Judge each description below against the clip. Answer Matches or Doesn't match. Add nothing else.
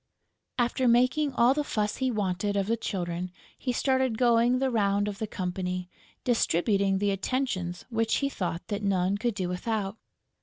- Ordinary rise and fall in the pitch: Matches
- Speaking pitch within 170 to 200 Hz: Doesn't match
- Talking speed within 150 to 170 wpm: Matches